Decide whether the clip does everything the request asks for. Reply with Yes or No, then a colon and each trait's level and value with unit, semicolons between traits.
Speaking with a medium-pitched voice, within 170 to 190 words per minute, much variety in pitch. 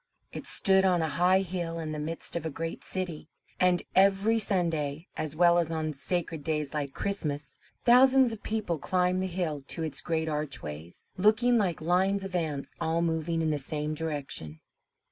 No: medium, 165 Hz; average, 180 wpm; average, 3.5 semitones